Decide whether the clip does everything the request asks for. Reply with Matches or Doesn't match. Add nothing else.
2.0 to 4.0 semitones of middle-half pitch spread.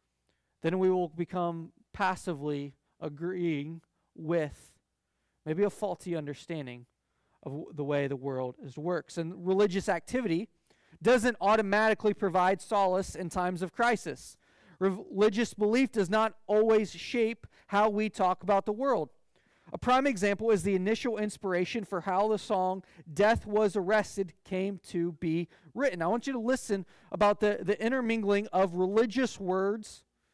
Matches